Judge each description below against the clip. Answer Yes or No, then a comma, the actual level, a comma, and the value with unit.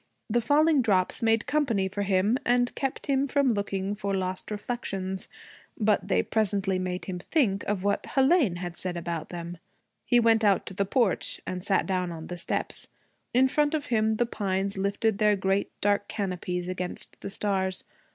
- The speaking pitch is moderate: No, high, 200 Hz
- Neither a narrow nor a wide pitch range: Yes, average, 3.8 semitones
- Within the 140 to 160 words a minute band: No, average, 180 wpm